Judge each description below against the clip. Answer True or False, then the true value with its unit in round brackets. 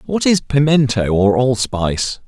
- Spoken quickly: False (130 wpm)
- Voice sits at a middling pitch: False (130 Hz)